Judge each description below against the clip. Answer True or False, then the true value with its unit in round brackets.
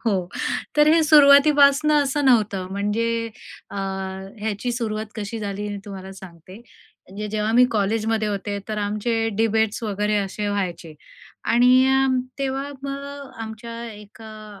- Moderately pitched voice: False (220 Hz)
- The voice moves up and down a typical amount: True (3.8 semitones)